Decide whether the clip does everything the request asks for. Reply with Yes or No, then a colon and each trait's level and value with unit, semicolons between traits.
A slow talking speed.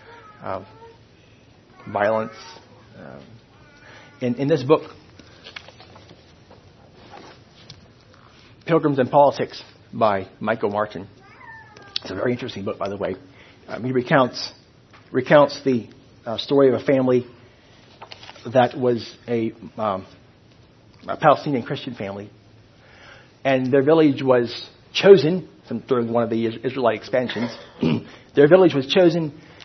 Yes: slow, 110 wpm